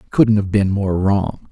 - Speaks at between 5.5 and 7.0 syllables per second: No, 5.1 syllables/s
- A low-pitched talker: Yes, low, 100 Hz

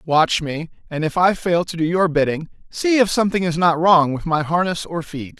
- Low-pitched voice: No, medium, 170 Hz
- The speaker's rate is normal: No, fast, 235 wpm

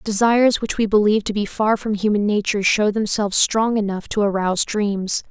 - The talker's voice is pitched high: Yes, high, 210 Hz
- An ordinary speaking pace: Yes, average, 190 wpm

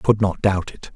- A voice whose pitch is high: No, low, 100 Hz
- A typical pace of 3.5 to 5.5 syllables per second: No, 5.9 syllables/s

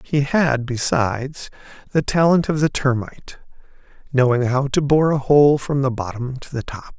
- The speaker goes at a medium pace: Yes, average, 165 wpm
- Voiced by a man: Yes, male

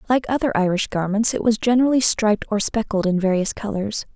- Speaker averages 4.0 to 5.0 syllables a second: No, 6.1 syllables/s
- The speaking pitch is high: Yes, high, 215 Hz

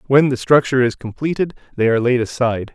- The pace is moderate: Yes, average, 195 wpm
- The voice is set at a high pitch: No, low, 125 Hz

